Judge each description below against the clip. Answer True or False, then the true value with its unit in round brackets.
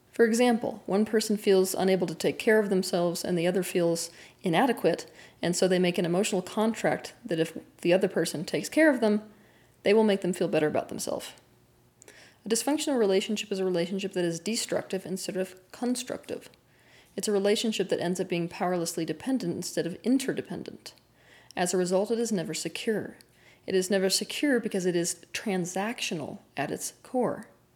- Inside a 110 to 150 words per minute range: False (175 wpm)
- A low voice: False (190 Hz)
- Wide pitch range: False (3.5 semitones)